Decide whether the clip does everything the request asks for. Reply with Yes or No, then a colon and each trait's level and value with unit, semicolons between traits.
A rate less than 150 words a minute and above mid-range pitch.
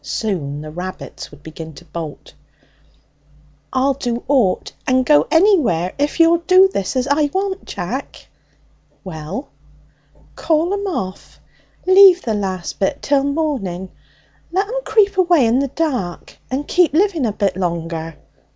Yes: average, 140 wpm; very high, 255 Hz